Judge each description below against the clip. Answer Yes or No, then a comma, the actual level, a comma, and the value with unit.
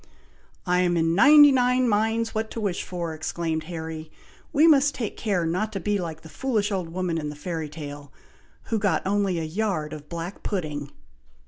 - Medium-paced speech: Yes, average, 190 wpm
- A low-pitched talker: No, medium, 180 Hz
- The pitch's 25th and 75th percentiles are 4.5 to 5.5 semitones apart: Yes, average, 5.2 semitones